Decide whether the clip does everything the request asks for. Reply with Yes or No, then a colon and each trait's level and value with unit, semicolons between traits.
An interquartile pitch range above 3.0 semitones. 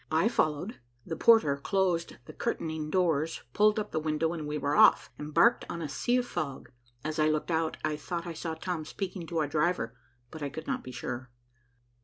No: average, 2.7 semitones